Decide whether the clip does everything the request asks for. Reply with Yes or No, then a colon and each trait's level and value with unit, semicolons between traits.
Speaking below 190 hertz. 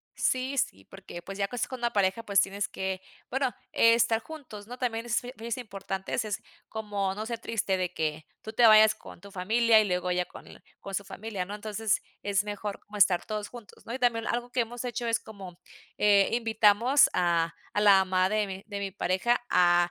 No: high, 210 Hz